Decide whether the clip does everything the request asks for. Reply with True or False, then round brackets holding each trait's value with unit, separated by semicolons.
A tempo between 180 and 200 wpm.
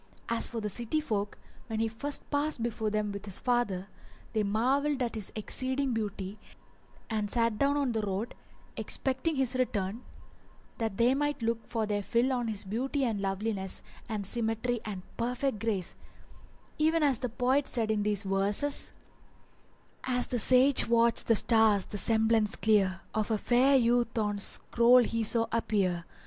False (165 wpm)